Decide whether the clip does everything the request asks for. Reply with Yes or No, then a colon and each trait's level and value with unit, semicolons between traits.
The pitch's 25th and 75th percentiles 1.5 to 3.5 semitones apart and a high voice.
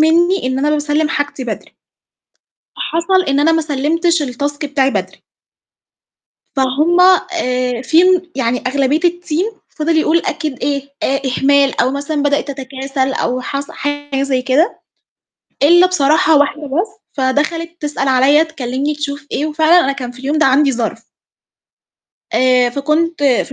Yes: average, 3.1 semitones; very high, 285 Hz